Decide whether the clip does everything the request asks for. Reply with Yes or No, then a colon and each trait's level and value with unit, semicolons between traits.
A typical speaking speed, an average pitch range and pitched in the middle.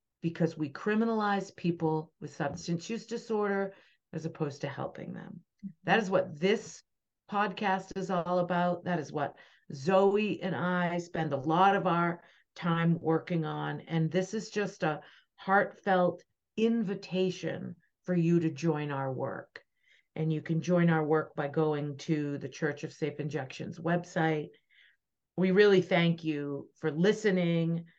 Yes: average, 150 wpm; average, 3.2 semitones; medium, 170 Hz